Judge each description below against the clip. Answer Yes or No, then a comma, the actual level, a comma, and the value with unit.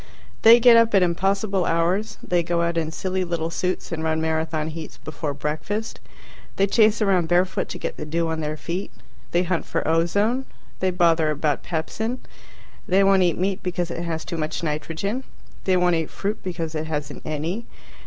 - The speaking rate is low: No, average, 185 wpm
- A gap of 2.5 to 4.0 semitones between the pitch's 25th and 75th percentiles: Yes, average, 3.3 semitones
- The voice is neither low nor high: Yes, medium, 170 Hz